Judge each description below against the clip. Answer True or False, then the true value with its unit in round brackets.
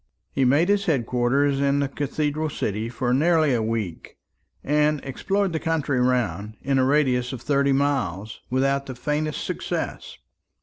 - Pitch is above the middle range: False (140 Hz)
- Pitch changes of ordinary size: True (3.1 semitones)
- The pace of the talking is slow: False (160 wpm)